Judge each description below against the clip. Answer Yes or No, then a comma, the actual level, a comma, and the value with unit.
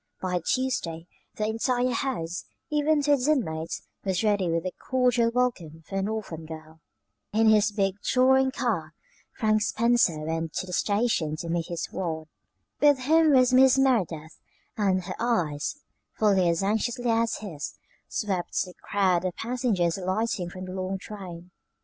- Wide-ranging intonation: Yes, wide, 6.0 semitones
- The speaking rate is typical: Yes, average, 155 wpm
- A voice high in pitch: Yes, high, 200 Hz